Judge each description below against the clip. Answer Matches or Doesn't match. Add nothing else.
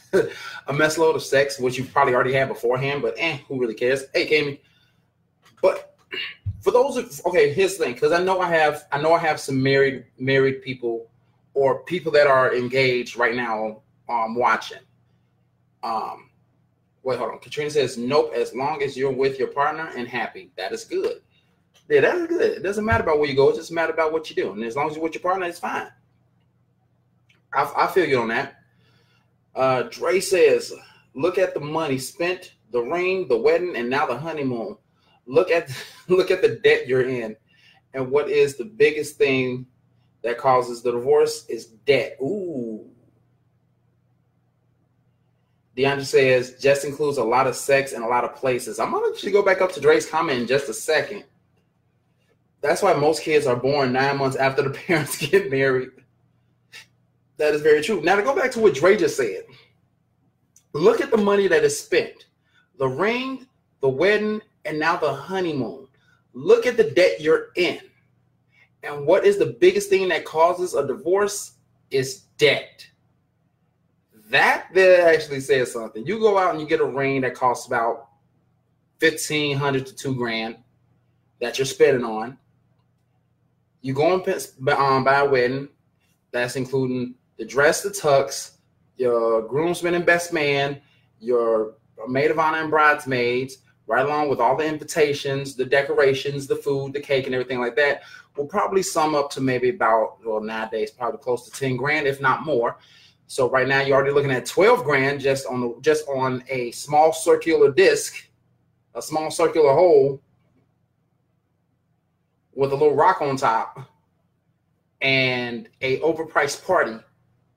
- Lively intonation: Matches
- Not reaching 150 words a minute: Doesn't match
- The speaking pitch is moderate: Matches